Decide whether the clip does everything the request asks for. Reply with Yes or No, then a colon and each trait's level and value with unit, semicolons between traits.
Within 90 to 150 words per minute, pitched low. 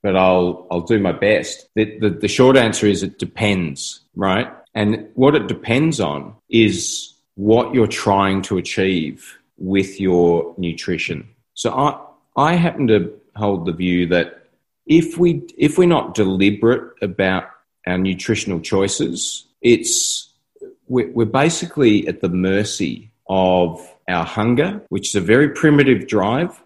Yes: average, 140 wpm; low, 105 Hz